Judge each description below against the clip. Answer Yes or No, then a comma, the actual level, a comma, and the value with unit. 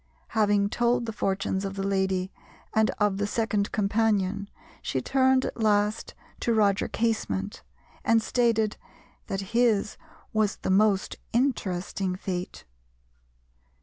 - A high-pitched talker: Yes, high, 205 Hz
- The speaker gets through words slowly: Yes, slow, 120 wpm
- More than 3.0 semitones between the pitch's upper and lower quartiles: No, narrow, 2.4 semitones